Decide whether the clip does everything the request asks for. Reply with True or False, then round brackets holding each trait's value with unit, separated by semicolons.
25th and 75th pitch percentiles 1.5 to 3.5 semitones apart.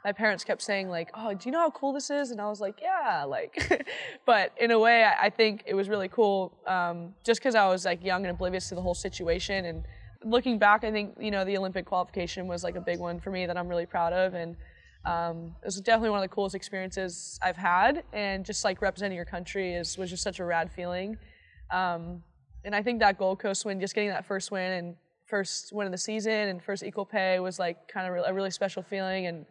True (2.6 semitones)